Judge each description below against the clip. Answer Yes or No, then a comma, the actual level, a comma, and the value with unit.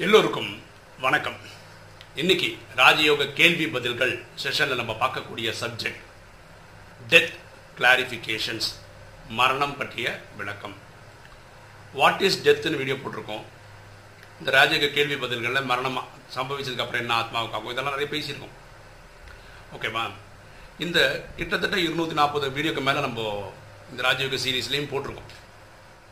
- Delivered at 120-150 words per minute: No, average, 100 wpm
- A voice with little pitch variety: No, average, 5.2 semitones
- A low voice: Yes, low, 120 Hz